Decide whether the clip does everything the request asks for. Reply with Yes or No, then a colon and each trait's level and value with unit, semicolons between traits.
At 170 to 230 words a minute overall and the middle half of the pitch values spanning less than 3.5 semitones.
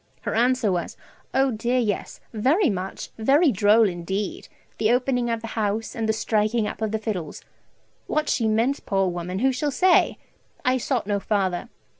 No: average, 175 wpm; average, 3.8 semitones